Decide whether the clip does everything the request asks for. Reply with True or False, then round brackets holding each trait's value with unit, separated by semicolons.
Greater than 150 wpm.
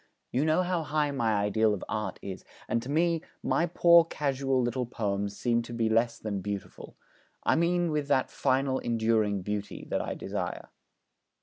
True (175 wpm)